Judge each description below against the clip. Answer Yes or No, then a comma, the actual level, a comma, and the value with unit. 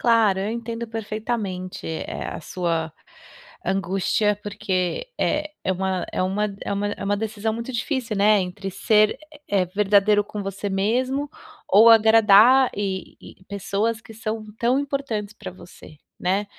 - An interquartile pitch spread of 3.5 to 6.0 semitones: No, average, 2.7 semitones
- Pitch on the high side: Yes, high, 210 Hz